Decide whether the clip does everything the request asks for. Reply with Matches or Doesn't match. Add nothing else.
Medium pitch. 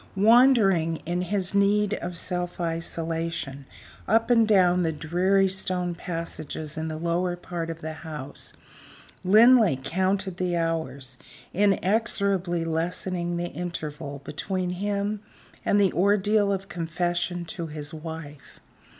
Matches